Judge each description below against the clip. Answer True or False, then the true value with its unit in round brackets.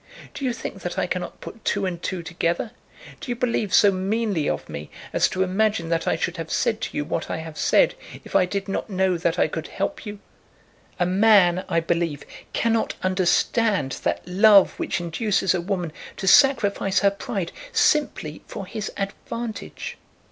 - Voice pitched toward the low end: False (190 Hz)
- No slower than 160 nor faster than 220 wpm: True (185 wpm)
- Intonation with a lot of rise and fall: False (3.8 semitones)